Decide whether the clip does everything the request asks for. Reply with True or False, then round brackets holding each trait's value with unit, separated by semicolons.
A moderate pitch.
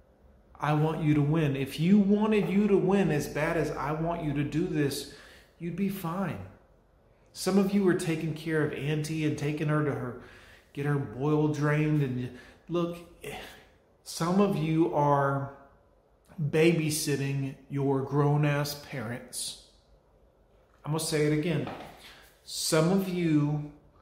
True (150 Hz)